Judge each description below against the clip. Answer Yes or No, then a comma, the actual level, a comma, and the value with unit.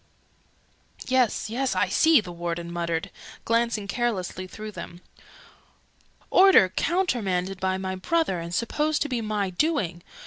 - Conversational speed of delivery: No, slow, 130 wpm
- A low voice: No, high, 205 Hz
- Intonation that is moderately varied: No, wide, 5.8 semitones